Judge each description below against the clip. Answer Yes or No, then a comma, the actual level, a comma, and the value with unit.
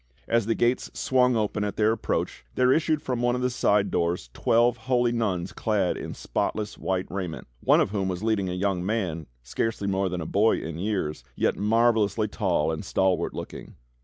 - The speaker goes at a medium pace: Yes, average, 190 wpm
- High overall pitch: No, low, 105 Hz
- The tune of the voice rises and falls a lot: No, average, 4.0 semitones